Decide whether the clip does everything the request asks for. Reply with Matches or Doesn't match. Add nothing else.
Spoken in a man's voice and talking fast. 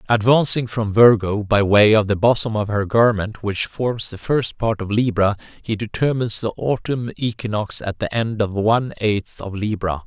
Doesn't match